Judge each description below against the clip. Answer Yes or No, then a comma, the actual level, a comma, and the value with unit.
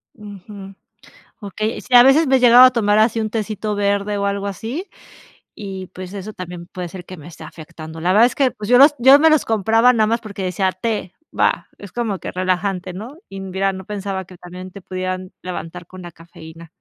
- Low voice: No, high, 200 Hz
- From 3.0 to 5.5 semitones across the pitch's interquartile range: Yes, average, 3.3 semitones